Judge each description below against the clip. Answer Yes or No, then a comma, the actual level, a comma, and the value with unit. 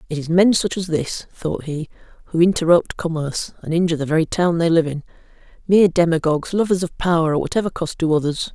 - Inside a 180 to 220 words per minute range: Yes, fast, 205 wpm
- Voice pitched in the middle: Yes, medium, 165 Hz